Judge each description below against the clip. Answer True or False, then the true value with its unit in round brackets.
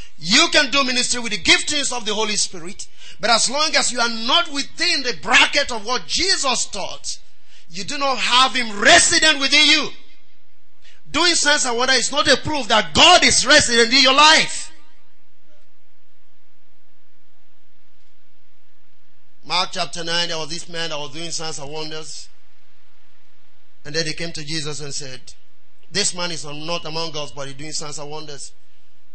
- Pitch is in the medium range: False (220 Hz)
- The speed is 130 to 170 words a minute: True (165 wpm)